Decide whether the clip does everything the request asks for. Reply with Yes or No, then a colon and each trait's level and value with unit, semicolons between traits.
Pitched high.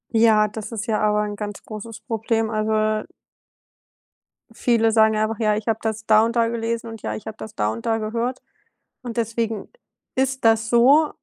Yes: high, 225 Hz